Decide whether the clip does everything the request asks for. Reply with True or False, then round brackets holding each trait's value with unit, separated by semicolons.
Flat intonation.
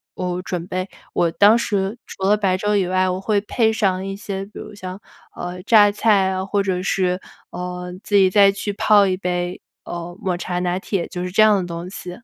True (2.1 semitones)